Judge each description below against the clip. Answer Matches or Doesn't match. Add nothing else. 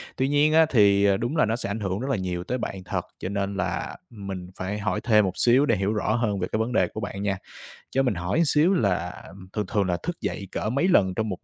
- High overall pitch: Doesn't match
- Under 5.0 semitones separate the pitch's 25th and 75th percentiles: Matches